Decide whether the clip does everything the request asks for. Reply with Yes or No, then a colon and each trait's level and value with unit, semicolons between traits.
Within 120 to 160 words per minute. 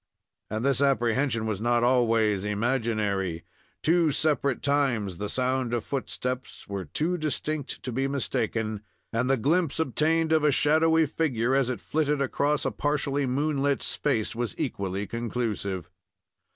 Yes: average, 140 wpm